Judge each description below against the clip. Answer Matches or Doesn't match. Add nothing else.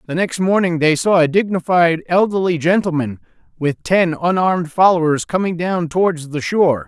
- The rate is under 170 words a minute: Matches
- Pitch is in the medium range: Matches